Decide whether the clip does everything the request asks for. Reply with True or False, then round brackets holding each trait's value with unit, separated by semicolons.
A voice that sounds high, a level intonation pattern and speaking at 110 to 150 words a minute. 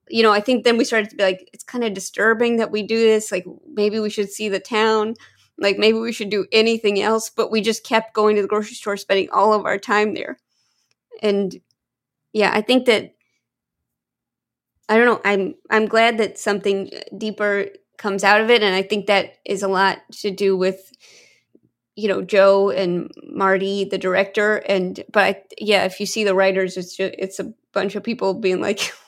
False (210 Hz; 2.3 semitones; 205 wpm)